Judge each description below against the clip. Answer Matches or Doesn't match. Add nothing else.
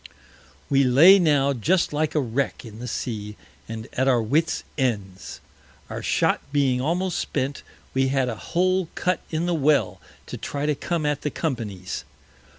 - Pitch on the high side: Doesn't match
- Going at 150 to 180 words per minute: Matches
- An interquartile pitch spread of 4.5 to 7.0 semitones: Matches